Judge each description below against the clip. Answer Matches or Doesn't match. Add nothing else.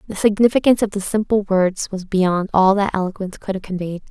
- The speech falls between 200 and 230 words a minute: Matches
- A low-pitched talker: Doesn't match